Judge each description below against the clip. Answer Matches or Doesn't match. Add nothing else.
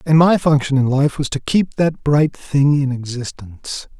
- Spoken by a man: Matches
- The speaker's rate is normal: Matches